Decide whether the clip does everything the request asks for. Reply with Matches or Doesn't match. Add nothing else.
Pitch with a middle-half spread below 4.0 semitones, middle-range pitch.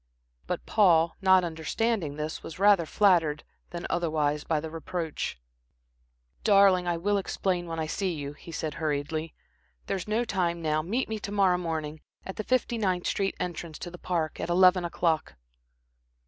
Matches